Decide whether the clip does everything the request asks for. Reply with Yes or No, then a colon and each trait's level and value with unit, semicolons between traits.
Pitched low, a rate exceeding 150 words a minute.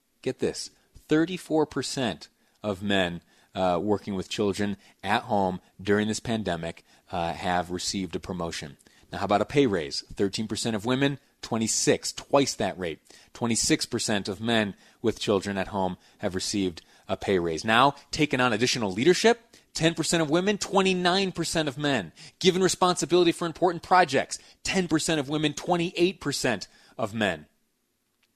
No: low, 120 Hz; average, 140 wpm